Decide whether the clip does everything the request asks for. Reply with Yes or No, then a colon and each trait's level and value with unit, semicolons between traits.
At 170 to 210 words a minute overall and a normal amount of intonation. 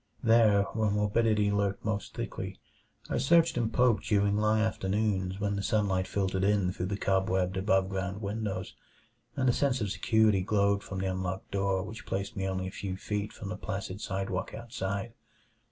No: average, 175 wpm; narrow, 2.2 semitones